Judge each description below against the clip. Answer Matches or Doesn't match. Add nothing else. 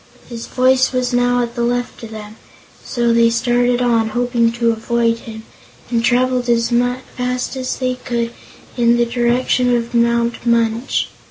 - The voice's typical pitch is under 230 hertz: Doesn't match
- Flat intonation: Matches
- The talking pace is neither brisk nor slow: Matches